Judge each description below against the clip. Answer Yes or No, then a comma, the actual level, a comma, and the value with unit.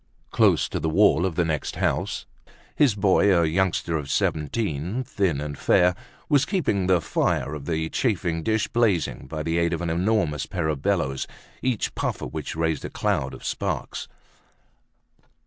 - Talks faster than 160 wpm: Yes, average, 170 wpm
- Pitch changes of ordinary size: Yes, average, 4.4 semitones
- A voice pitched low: Yes, very low, 85 Hz